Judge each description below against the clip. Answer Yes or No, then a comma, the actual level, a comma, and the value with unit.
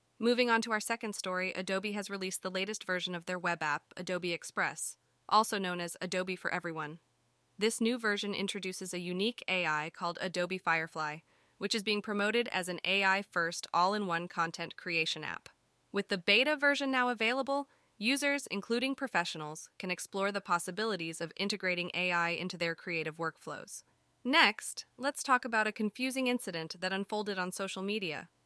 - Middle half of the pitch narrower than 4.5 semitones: Yes, average, 3.8 semitones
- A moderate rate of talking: Yes, average, 170 wpm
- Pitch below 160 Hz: No, high, 190 Hz